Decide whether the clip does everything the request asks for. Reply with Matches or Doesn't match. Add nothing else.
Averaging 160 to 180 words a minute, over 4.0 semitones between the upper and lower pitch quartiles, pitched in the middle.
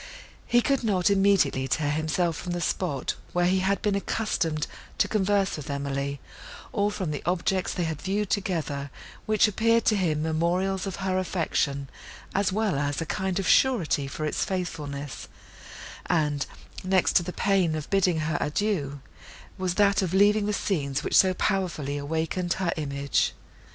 Matches